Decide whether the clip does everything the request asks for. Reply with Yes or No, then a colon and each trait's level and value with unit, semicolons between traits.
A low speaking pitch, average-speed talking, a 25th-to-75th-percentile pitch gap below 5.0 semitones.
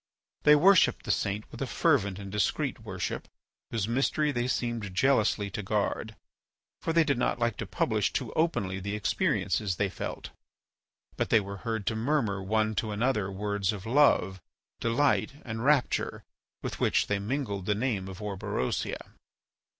Yes: low, 110 Hz; average, 160 wpm; average, 4.1 semitones